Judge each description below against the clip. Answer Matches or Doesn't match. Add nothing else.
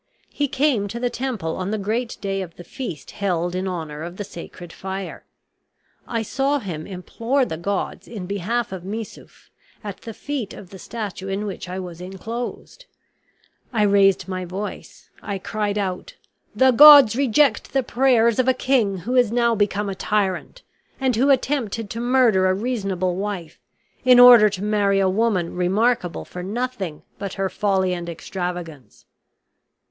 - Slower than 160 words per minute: Doesn't match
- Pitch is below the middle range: Doesn't match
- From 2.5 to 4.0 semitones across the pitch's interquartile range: Doesn't match